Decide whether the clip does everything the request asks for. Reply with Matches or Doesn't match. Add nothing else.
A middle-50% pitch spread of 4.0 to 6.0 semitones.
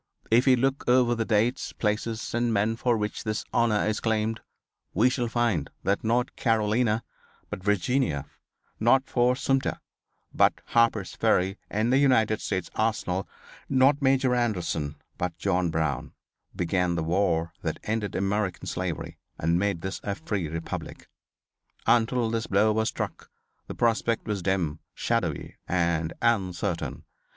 Matches